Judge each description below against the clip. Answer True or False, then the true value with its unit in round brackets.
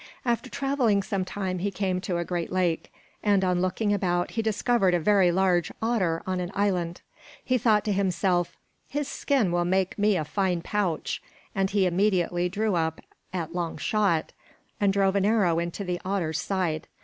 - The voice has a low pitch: False (190 Hz)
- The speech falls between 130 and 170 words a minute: False (180 wpm)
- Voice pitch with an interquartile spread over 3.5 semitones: False (2.7 semitones)